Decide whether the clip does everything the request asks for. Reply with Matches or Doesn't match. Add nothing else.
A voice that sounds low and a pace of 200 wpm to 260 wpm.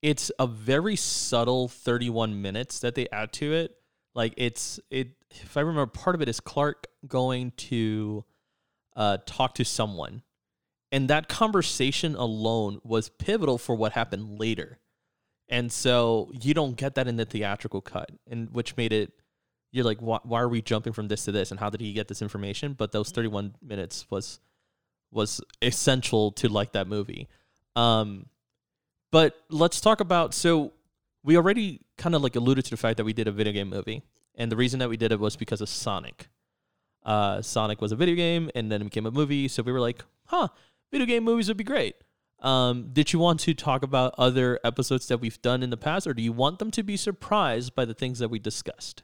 Matches